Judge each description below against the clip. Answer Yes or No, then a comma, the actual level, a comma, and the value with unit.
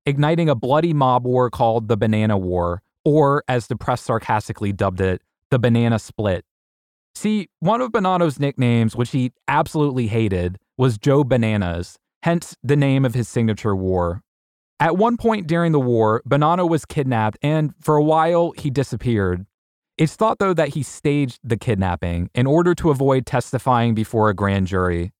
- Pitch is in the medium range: No, low, 125 Hz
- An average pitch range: No, wide, 5.8 semitones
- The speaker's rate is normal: Yes, average, 165 wpm